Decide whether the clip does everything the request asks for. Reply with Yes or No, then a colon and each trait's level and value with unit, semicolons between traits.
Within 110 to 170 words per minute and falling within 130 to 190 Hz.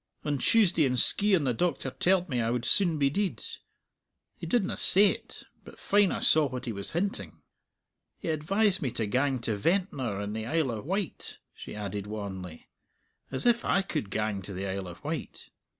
No: average, 185 wpm; low, 135 Hz